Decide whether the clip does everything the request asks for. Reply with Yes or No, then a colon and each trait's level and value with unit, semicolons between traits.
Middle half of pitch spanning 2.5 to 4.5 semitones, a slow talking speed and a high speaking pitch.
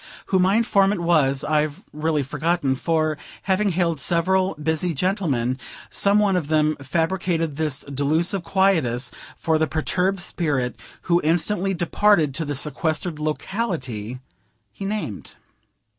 No: average, 4.1 semitones; slow, 130 wpm; medium, 160 Hz